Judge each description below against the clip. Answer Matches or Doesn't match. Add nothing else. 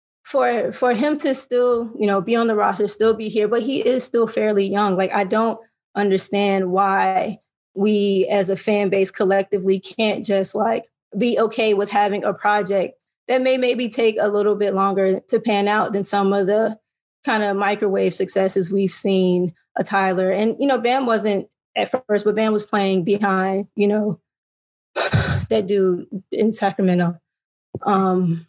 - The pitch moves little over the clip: Matches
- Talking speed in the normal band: Matches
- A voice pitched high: Matches